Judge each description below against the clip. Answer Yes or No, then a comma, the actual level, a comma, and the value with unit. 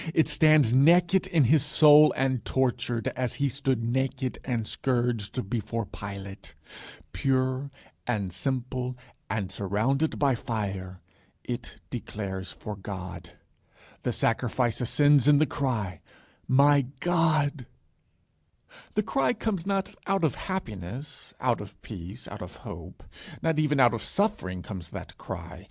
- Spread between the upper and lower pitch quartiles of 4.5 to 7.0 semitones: Yes, wide, 5.6 semitones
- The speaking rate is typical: No, slow, 130 wpm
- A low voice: Yes, low, 130 Hz